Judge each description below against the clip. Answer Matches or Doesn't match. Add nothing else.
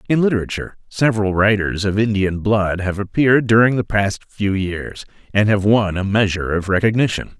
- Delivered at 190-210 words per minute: Doesn't match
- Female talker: Doesn't match